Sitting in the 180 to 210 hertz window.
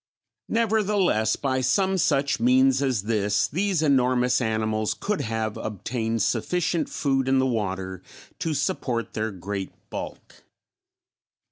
No: low, 125 Hz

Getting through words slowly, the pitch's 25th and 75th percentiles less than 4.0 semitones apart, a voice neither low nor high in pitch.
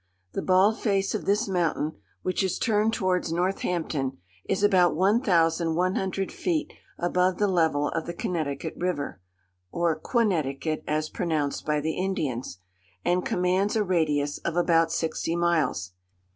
No: average, 145 wpm; average, 3.3 semitones; medium, 175 Hz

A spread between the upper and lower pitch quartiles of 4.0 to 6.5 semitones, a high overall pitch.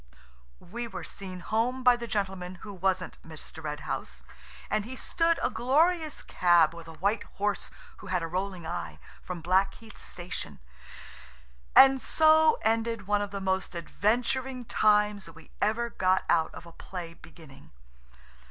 Yes: average, 5.1 semitones; high, 200 Hz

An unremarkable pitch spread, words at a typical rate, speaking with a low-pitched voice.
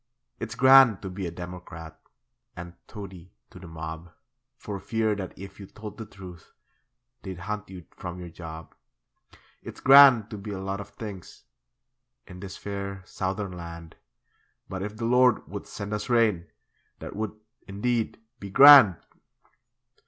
Yes: average, 3.2 semitones; average, 150 wpm; low, 100 Hz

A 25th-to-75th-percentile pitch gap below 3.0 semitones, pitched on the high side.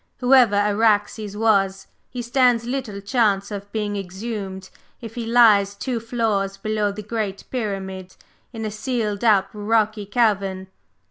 Yes: narrow, 2.5 semitones; high, 210 Hz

